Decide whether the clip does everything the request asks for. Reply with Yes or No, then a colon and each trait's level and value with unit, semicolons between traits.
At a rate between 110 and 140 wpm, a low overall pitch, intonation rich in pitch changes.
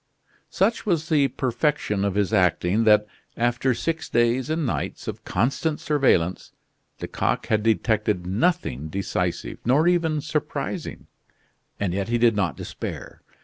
Yes: slow, 135 wpm; low, 120 Hz; wide, 7.0 semitones